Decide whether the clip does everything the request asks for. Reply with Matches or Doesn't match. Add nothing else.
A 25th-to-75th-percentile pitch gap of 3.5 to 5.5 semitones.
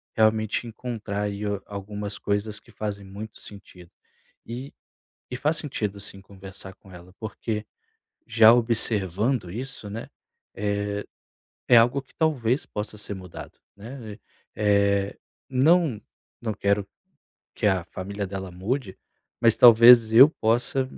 Doesn't match